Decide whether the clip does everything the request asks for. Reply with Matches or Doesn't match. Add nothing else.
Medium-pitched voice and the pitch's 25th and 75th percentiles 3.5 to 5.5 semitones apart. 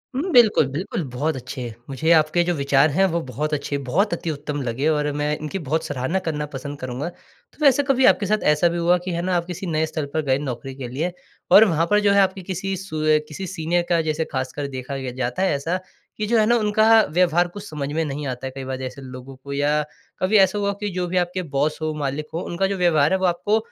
Matches